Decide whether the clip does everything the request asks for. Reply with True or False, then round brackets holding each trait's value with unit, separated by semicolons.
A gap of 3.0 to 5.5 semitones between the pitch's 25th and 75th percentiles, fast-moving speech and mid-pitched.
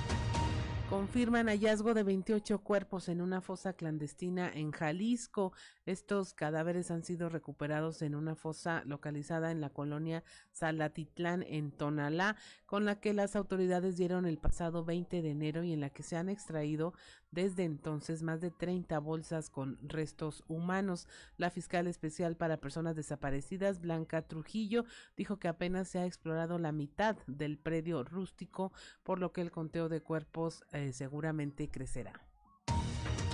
False (3.4 semitones; 150 wpm; 165 Hz)